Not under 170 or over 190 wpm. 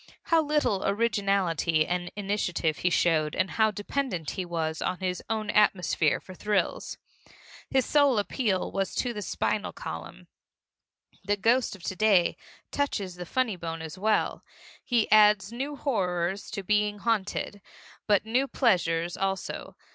No: average, 145 wpm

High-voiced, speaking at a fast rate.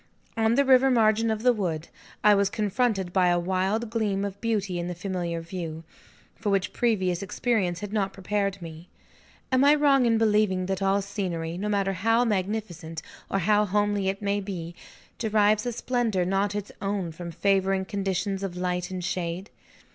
No: high, 195 Hz; average, 175 wpm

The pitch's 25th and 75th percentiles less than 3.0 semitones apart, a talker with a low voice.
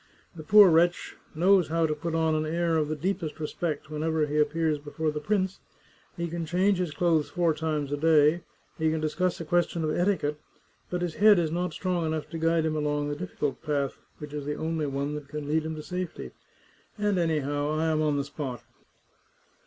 No: narrow, 2.4 semitones; medium, 160 Hz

